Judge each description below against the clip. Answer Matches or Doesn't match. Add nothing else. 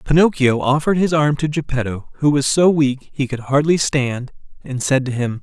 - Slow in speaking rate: Doesn't match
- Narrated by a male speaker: Matches